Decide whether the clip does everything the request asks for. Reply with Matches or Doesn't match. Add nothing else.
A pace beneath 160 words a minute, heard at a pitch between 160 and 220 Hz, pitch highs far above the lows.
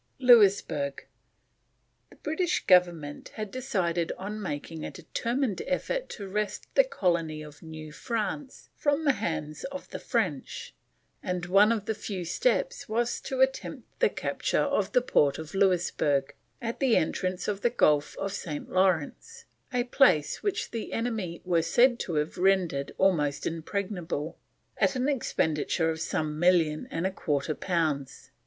Matches